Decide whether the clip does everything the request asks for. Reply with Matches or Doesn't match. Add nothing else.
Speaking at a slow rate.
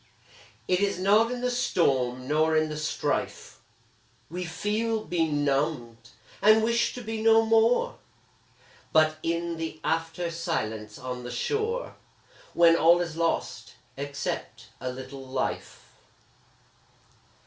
Matches